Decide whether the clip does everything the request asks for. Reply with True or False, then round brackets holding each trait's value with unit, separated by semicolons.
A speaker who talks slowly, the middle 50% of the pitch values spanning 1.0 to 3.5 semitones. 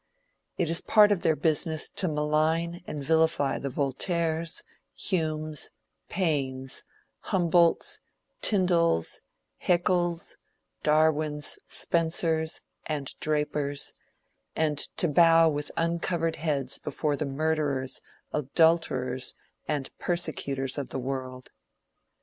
True (100 wpm; 2.9 semitones)